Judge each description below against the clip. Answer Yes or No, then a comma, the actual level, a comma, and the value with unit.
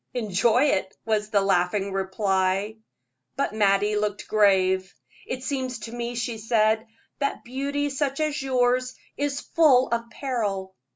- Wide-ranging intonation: No, average, 4.5 semitones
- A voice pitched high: Yes, high, 225 Hz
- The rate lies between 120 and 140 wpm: Yes, slow, 135 wpm